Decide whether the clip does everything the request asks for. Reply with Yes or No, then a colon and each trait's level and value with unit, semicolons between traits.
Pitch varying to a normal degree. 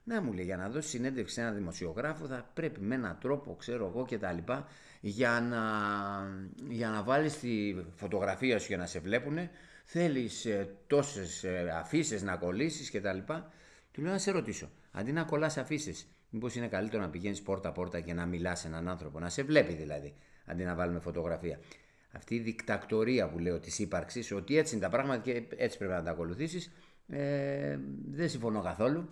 No: wide, 7.1 semitones